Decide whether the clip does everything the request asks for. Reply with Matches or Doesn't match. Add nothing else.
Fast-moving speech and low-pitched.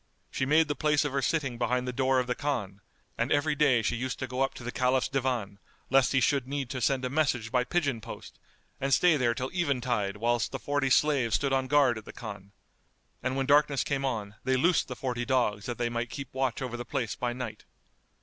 Matches